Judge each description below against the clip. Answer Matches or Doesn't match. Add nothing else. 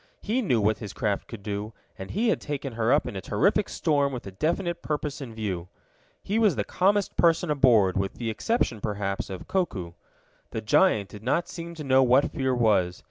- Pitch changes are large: Matches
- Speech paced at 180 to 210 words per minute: Matches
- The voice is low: Matches